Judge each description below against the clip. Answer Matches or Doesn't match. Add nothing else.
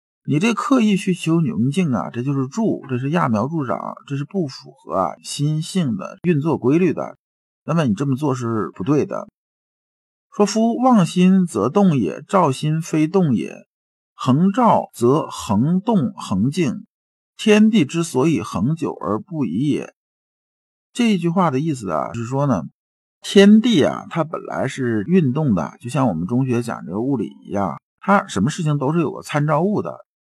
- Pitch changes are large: Matches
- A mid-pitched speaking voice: Matches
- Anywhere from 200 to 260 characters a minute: Matches